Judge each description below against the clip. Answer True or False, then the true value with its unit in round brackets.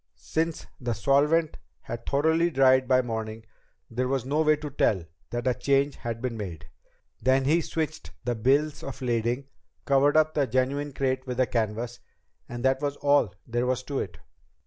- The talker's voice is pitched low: True (130 Hz)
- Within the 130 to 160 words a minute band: False (175 wpm)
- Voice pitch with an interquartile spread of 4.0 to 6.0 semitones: False (3.2 semitones)